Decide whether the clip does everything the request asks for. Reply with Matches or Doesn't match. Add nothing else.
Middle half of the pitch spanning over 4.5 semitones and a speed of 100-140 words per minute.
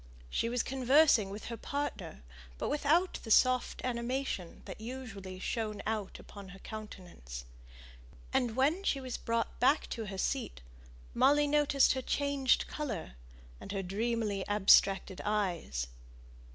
Matches